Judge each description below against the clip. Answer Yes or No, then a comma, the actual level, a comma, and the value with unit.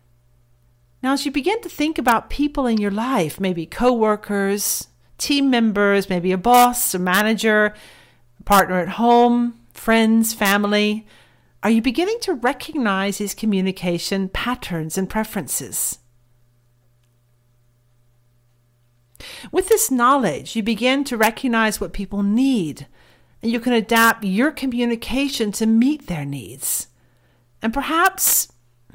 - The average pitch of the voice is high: Yes, high, 210 Hz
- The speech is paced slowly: Yes, slow, 120 wpm